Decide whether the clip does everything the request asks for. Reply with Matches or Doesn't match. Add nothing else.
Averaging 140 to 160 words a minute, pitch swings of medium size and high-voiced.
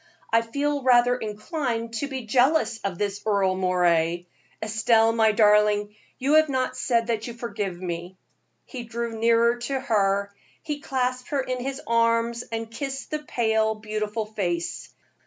Matches